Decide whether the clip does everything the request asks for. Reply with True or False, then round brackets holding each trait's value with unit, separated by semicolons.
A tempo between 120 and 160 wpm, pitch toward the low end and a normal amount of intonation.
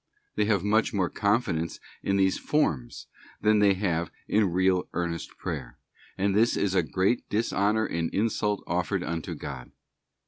True (150 wpm; 95 Hz; 3.5 semitones)